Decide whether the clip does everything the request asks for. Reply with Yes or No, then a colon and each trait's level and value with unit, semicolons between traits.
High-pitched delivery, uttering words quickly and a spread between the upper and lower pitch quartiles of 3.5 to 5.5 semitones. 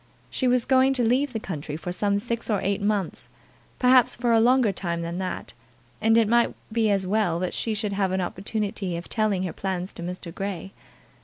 Yes: high, 205 Hz; fast, 210 wpm; average, 4.0 semitones